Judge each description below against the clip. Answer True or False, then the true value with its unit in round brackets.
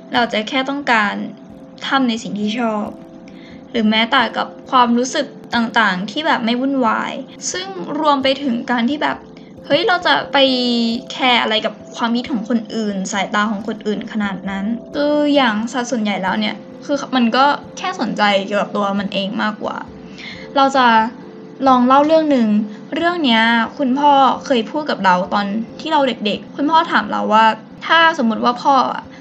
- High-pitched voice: True (240 Hz)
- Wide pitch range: False (4.0 semitones)